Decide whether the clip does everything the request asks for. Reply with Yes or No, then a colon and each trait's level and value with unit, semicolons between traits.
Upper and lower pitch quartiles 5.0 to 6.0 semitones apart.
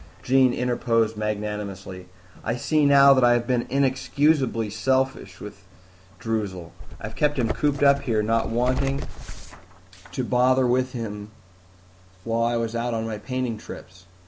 No: average, 3.3 semitones